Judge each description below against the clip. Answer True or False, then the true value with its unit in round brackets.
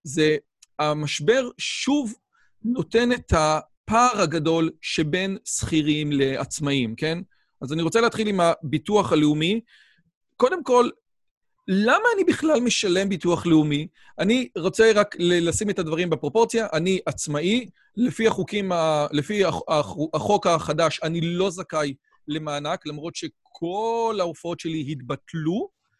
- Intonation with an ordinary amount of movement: False (5.7 semitones)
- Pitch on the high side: False (170 Hz)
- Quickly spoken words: False (115 wpm)